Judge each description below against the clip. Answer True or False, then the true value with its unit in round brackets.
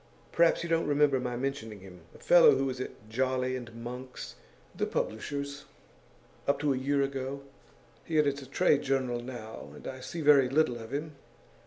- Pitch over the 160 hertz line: False (135 Hz)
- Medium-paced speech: True (180 wpm)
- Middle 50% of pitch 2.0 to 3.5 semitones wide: True (2.4 semitones)